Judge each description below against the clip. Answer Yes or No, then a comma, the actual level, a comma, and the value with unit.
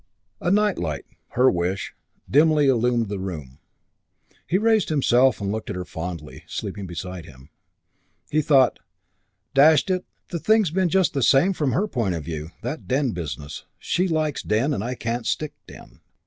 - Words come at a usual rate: Yes, average, 170 wpm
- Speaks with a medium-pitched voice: No, low, 125 Hz